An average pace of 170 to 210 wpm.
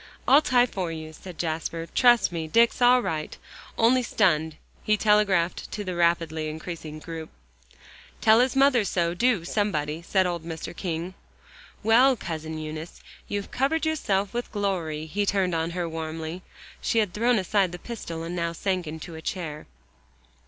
No: average, 160 wpm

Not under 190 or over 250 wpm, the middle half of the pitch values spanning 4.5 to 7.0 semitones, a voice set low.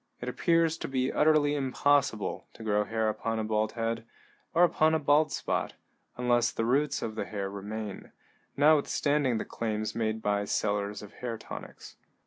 No: average, 165 wpm; average, 5.0 semitones; low, 115 Hz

